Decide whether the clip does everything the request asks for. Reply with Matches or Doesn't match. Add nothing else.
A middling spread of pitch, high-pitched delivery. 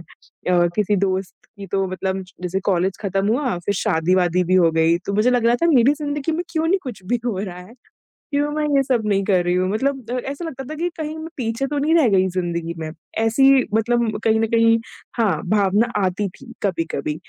Doesn't match